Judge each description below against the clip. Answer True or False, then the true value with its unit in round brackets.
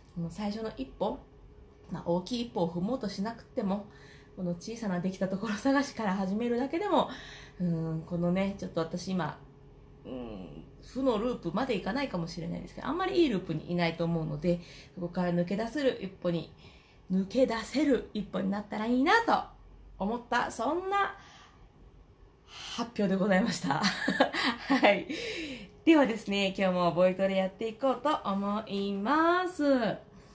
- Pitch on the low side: False (200 Hz)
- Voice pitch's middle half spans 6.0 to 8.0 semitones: False (5.6 semitones)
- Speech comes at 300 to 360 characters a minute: True (315 characters per minute)